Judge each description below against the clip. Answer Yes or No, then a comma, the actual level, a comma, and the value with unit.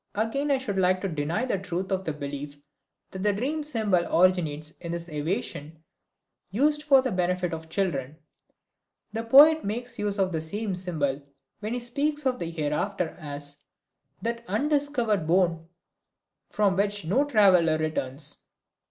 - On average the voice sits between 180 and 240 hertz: Yes, medium, 185 Hz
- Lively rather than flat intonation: Yes, wide, 6.3 semitones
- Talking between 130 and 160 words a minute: Yes, average, 150 wpm